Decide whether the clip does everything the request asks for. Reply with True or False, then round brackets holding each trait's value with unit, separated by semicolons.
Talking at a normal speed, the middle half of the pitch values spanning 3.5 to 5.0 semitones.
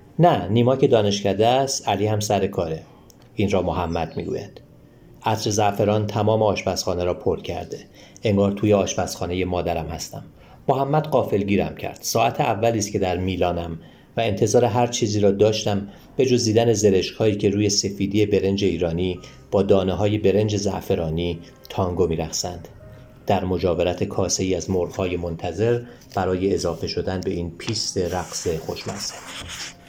False (145 wpm; 3.1 semitones)